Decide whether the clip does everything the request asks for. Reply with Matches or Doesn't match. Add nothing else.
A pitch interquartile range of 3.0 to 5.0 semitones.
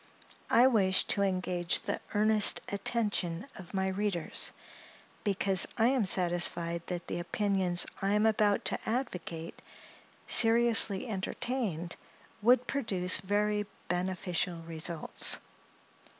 Matches